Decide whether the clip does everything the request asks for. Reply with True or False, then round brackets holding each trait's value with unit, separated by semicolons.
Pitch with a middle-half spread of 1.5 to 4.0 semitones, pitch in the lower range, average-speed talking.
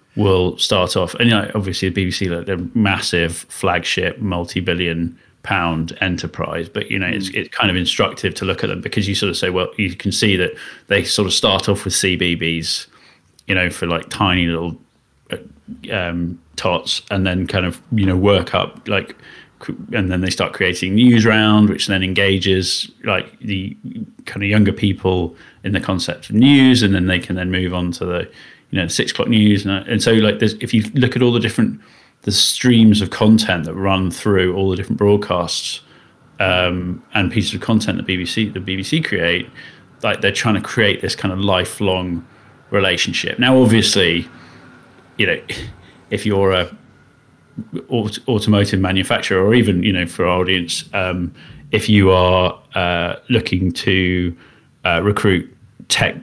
True (2.7 semitones; 95 Hz; 180 wpm)